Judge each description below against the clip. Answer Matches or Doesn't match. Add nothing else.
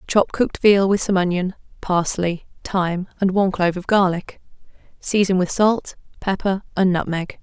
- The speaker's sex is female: Matches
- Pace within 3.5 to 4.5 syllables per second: Doesn't match